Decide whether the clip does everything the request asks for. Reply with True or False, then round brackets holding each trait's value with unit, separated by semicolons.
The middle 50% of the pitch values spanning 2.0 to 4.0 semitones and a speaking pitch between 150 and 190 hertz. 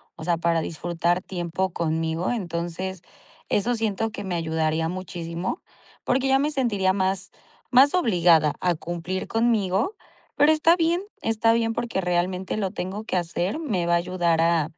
False (4.8 semitones; 185 Hz)